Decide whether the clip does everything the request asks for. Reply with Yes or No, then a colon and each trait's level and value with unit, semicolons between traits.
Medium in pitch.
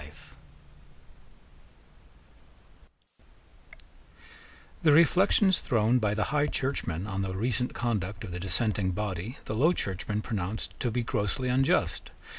No: low, 110 Hz